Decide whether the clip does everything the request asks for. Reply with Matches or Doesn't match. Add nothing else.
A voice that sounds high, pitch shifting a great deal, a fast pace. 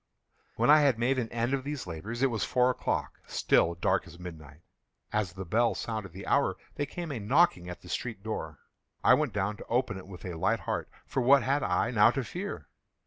Doesn't match